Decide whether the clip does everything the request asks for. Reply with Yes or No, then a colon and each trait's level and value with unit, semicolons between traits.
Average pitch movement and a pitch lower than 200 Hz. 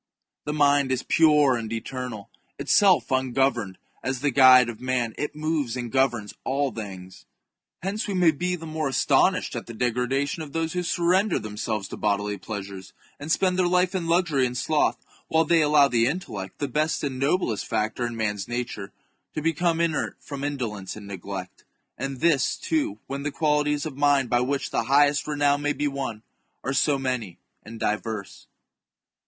Yes: average, 4.8 semitones; low, 135 Hz